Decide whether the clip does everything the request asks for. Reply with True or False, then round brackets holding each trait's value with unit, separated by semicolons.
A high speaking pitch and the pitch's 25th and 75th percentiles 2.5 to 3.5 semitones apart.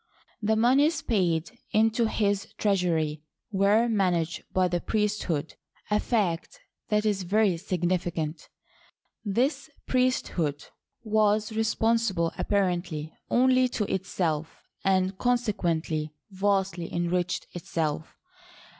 False (195 Hz; 4.2 semitones)